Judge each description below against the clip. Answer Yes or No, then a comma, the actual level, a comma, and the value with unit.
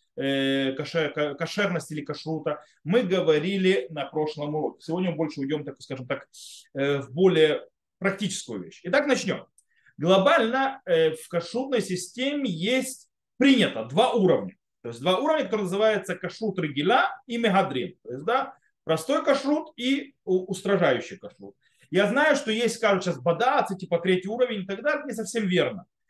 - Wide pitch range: Yes, wide, 7.6 semitones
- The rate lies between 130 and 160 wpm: Yes, average, 145 wpm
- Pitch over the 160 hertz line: Yes, high, 190 Hz